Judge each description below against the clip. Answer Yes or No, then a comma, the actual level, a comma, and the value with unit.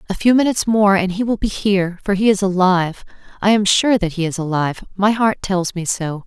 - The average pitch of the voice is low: No, high, 195 Hz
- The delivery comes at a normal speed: No, fast, 240 wpm